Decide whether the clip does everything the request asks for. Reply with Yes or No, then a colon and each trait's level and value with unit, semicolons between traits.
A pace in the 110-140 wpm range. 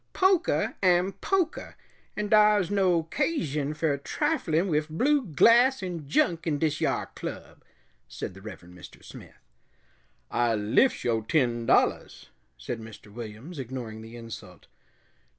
Yes: slow, 135 wpm